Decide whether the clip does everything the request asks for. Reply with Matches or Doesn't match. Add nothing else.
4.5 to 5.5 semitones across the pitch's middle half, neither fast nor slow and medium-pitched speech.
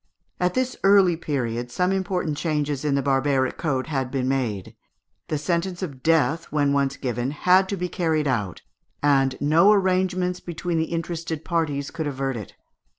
Matches